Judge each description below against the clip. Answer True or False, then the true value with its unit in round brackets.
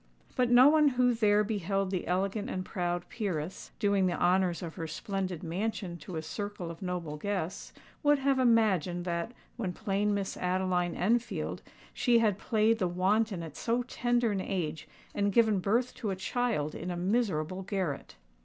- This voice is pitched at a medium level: False (195 Hz)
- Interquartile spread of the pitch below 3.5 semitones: False (4.2 semitones)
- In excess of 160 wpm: True (170 wpm)